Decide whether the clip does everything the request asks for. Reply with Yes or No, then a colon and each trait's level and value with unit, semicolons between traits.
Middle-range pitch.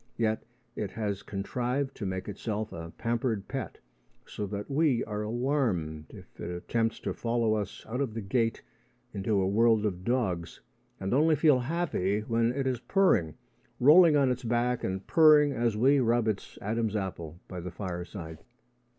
No: low, 115 Hz